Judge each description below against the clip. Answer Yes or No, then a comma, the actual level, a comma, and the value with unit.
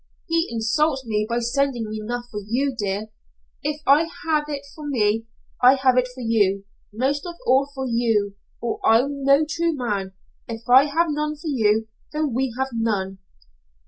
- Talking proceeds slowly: No, average, 175 wpm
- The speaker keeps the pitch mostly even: No, average, 4.3 semitones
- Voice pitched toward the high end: Yes, very high, 250 Hz